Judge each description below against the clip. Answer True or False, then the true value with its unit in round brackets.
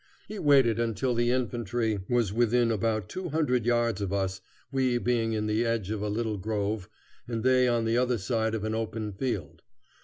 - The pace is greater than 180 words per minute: True (190 wpm)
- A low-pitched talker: True (115 Hz)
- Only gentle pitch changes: True (2.3 semitones)